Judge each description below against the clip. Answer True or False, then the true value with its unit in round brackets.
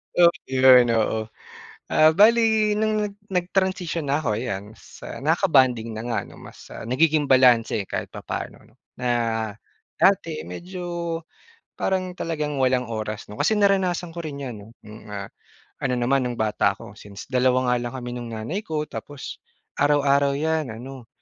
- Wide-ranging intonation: True (6.1 semitones)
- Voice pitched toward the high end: False (135 Hz)